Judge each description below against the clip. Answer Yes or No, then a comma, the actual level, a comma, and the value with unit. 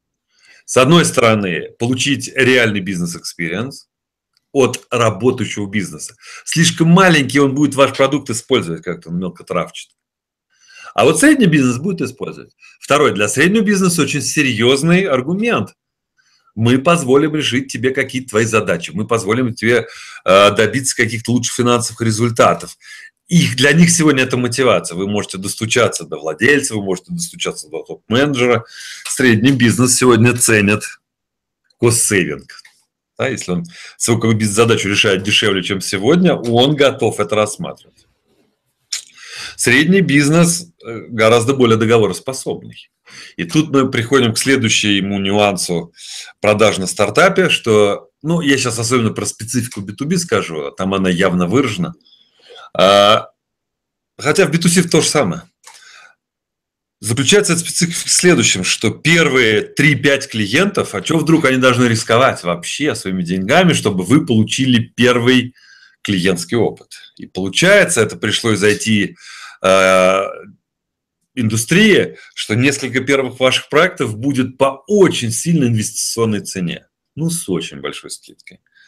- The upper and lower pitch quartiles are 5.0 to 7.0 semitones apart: Yes, wide, 5.5 semitones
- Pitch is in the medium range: No, low, 125 Hz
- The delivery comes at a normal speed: Yes, average, 125 wpm